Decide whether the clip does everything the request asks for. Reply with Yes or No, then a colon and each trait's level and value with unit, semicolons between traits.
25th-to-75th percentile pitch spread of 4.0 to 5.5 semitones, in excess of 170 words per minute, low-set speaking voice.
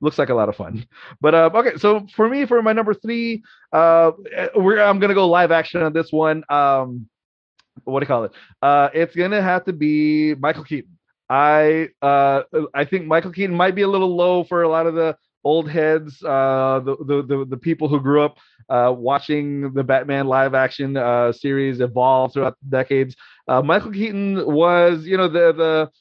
No: average, 4.4 semitones; average, 200 wpm; medium, 155 Hz